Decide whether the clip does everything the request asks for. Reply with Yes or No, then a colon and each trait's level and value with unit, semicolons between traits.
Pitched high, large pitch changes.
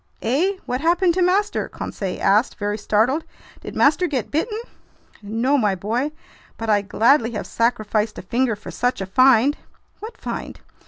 Yes: high, 245 Hz; wide, 6.0 semitones